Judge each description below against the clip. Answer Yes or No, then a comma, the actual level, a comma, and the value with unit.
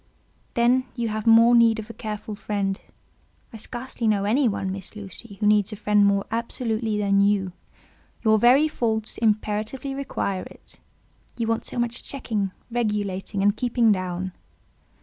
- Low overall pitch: No, high, 215 Hz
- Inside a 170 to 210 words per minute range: No, average, 155 wpm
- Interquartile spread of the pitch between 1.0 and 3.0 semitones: Yes, narrow, 2.6 semitones